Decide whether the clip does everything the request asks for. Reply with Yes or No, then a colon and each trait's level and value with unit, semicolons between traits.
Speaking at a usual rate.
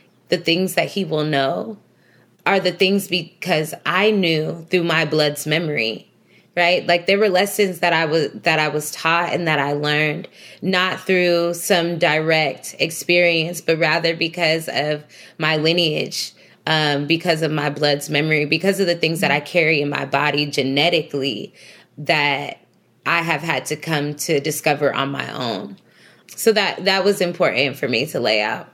Yes: average, 170 wpm